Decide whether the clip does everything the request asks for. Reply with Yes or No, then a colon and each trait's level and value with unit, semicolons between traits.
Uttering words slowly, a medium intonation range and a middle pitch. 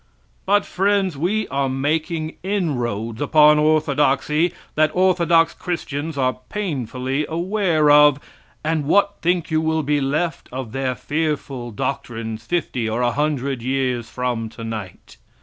Yes: slow, 130 wpm; average, 4.4 semitones; medium, 150 Hz